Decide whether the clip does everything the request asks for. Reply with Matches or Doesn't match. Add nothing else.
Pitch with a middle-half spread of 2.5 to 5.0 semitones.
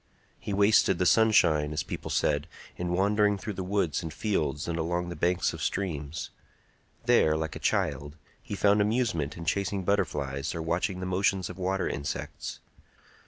Matches